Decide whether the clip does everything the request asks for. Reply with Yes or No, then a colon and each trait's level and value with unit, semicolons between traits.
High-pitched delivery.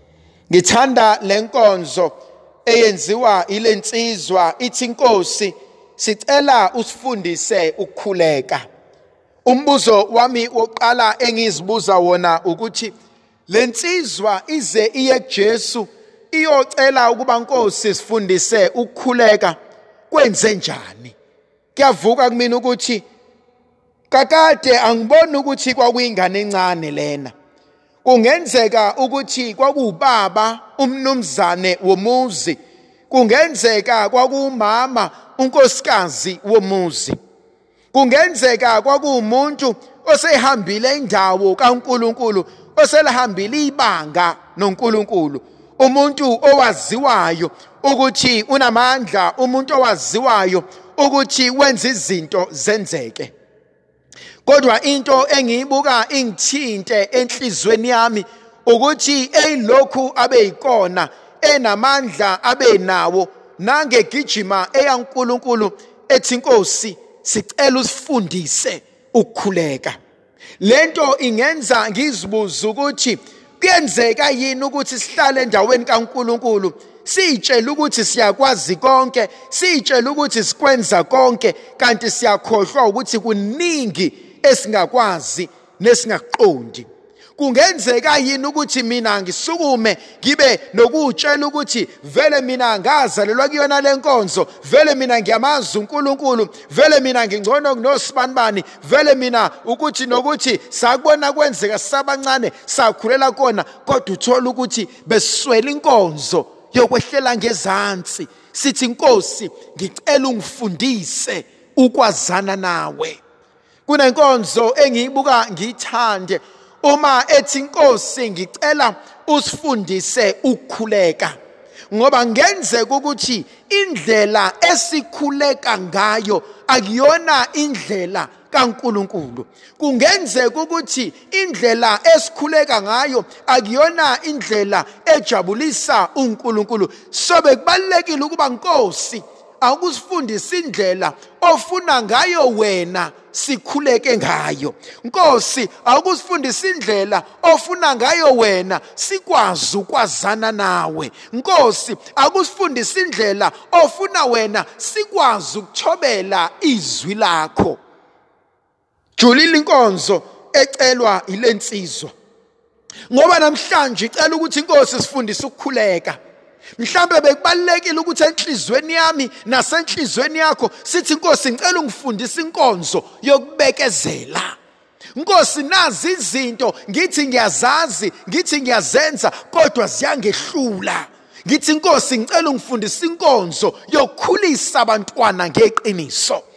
Yes: very high, 255 Hz